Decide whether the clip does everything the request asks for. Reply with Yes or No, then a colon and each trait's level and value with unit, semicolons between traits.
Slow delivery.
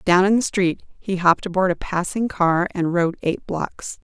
No: fast, 205 wpm